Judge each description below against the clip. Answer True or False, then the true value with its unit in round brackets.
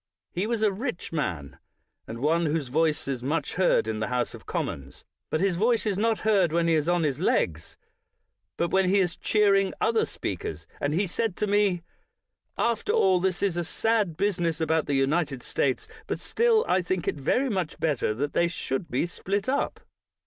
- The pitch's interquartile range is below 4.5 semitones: False (5.6 semitones)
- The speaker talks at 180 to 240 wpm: True (195 wpm)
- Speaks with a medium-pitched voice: True (175 Hz)